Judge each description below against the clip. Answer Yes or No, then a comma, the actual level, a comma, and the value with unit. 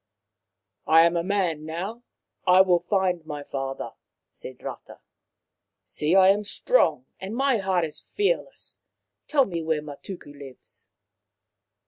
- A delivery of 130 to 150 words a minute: Yes, average, 140 wpm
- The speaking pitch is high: No, medium, 180 Hz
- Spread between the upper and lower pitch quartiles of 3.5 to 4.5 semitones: Yes, average, 4.1 semitones